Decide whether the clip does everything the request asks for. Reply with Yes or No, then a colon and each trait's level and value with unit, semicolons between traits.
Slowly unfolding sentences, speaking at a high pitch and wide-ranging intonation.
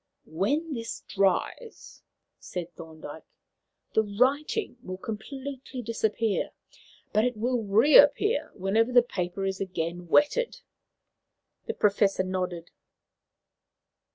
Yes: slow, 100 wpm; high, 215 Hz; wide, 5.7 semitones